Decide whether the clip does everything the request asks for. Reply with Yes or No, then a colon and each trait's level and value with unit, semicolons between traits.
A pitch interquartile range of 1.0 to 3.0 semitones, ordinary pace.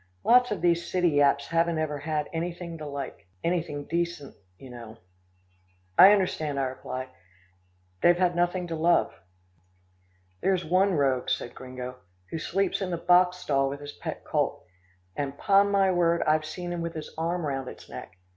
No: average, 3.9 semitones; average, 165 wpm